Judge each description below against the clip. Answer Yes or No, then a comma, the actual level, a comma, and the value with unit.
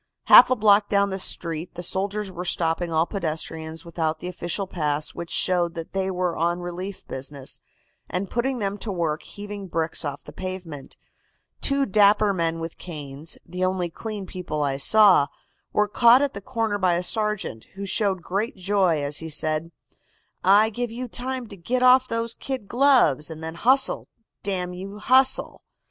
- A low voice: No, medium, 185 Hz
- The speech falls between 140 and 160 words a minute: No, average, 175 wpm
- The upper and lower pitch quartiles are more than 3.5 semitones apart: Yes, average, 4.2 semitones